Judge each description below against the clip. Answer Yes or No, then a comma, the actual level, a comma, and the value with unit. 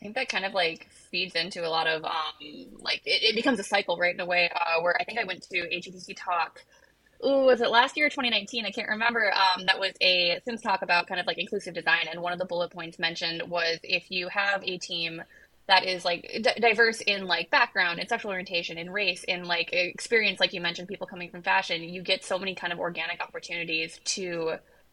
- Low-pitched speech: No, medium, 180 Hz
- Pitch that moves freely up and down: No, narrow, 2.6 semitones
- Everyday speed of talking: No, fast, 235 wpm